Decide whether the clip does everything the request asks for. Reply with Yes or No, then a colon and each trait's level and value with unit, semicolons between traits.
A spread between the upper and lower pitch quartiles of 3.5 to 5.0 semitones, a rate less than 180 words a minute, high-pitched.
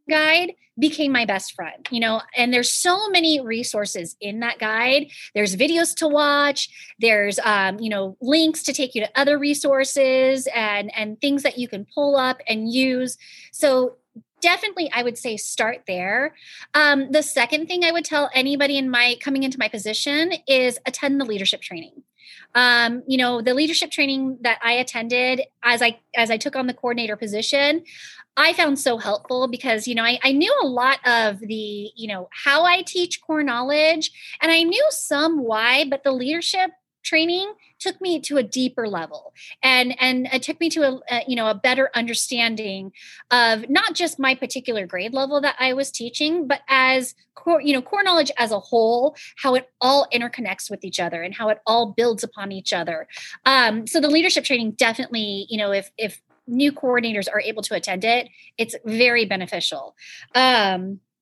No: average, 4.3 semitones; average, 185 wpm; very high, 255 Hz